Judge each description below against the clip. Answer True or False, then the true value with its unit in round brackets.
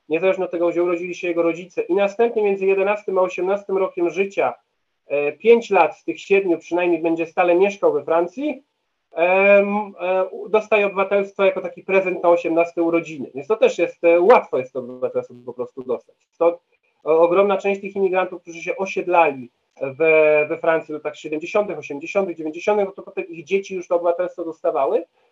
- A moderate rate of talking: False (170 wpm)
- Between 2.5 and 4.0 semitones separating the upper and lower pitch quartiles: True (3.2 semitones)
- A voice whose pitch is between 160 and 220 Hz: True (185 Hz)